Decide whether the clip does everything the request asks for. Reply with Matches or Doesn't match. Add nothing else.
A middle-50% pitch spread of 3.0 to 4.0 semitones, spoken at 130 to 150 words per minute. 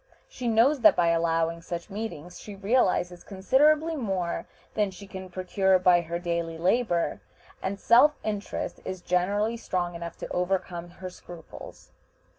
Matches